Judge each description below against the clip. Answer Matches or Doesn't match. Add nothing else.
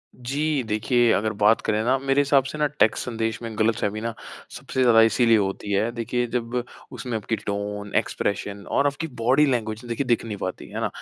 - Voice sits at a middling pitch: Doesn't match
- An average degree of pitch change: Matches